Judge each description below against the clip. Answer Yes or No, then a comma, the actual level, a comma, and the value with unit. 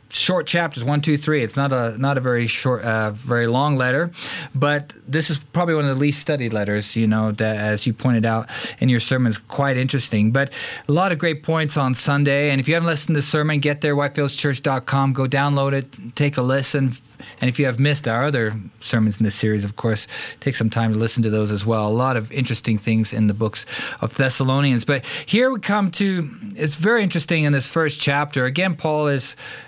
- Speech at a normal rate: No, fast, 220 wpm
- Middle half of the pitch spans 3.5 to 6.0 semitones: Yes, average, 4.4 semitones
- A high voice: No, low, 135 Hz